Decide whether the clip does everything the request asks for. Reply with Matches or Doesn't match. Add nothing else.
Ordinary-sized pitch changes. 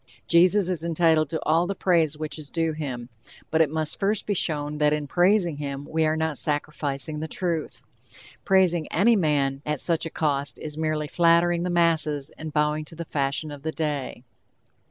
Doesn't match